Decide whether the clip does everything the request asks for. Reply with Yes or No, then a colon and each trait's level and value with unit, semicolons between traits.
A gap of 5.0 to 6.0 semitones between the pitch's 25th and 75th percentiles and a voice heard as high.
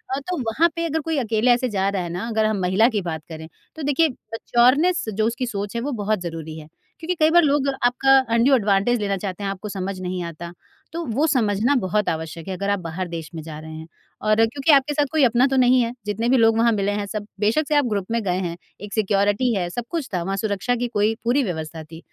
Yes: average, 5.3 semitones; high, 215 Hz